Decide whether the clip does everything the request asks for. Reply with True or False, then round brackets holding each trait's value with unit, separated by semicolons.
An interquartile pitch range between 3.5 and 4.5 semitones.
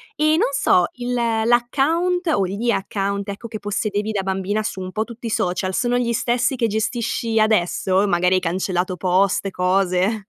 True (3.9 semitones)